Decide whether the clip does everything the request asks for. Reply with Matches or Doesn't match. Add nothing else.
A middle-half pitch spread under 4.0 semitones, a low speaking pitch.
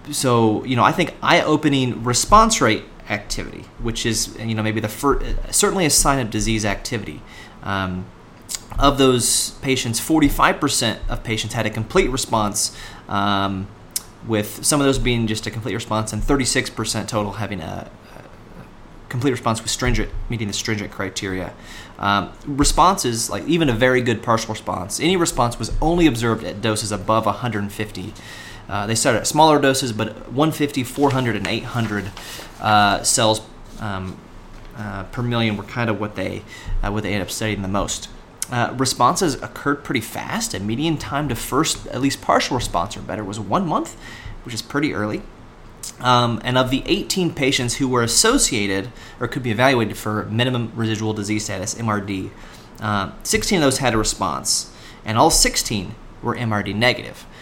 Matches